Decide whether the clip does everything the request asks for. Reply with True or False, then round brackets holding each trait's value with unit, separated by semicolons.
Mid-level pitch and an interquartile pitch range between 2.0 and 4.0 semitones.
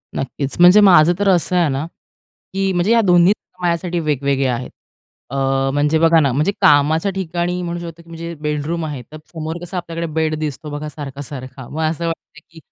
True (160 Hz; 2.9 semitones)